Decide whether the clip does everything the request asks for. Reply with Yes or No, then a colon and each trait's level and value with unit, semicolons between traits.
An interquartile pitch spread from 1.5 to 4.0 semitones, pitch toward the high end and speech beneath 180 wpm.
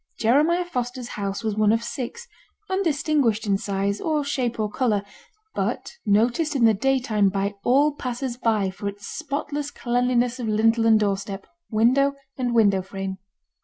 No: average, 4.9 semitones; high, 235 Hz; average, 155 wpm